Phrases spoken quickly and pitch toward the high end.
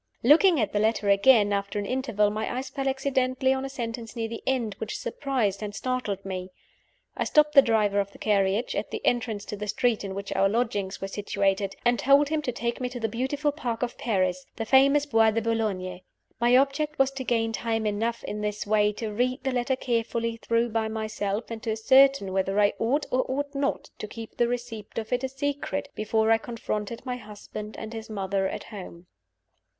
Yes: fast, 210 wpm; high, 225 Hz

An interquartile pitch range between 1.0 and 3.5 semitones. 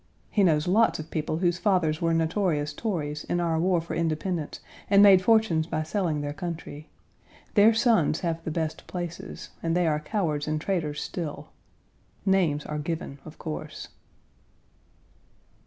Yes: average, 3.1 semitones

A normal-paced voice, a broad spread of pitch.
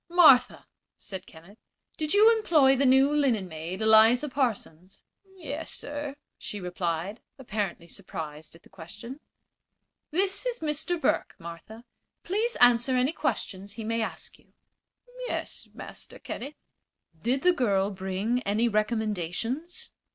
No: slow, 130 wpm; wide, 7.1 semitones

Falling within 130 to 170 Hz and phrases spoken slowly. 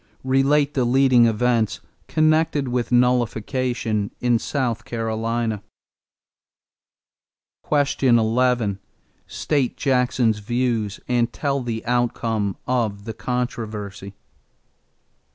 No: low, 120 Hz; slow, 80 wpm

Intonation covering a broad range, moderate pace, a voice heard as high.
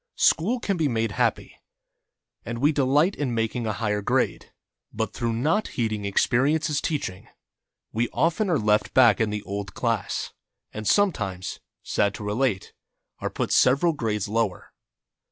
No: wide, 5.9 semitones; average, 155 wpm; low, 115 Hz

